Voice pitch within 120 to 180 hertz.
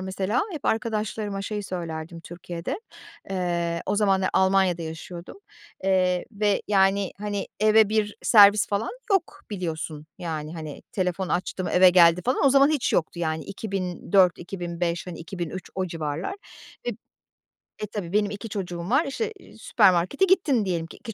No: high, 190 Hz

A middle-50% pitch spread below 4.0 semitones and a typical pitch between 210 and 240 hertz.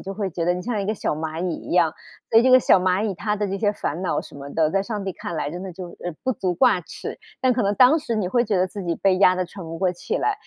No: average, 3.4 semitones; high, 190 Hz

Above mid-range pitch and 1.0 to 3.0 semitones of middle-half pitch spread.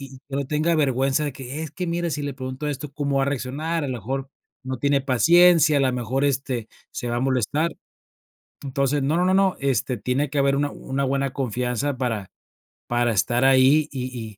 No: low, 135 Hz; narrow, 2.4 semitones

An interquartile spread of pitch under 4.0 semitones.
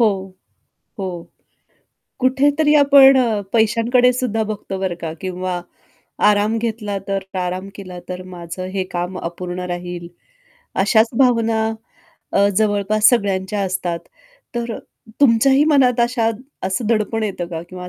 No: average, 4.3 semitones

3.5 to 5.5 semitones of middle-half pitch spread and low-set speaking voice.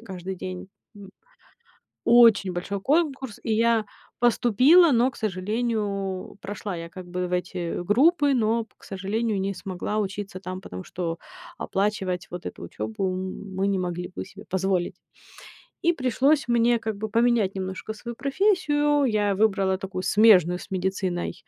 No: average, 3.9 semitones; high, 200 Hz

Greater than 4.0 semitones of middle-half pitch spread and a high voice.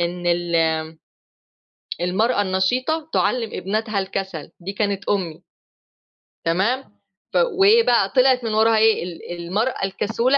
Yes: average, 4.8 semitones; high, 200 Hz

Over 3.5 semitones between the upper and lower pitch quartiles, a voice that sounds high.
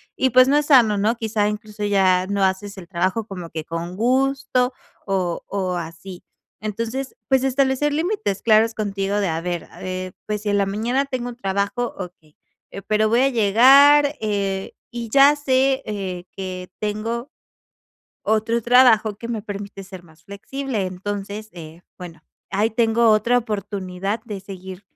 Yes: average, 4.2 semitones; high, 210 Hz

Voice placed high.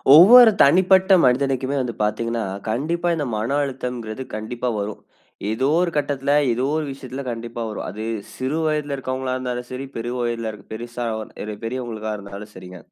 No: low, 125 Hz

